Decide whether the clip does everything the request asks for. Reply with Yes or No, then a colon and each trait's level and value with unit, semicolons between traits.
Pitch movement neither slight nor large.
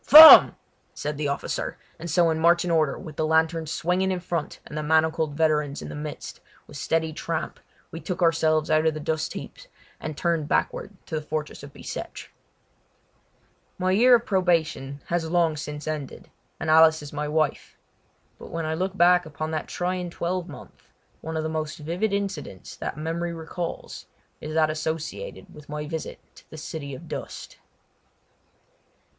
No: narrow, 2.0 semitones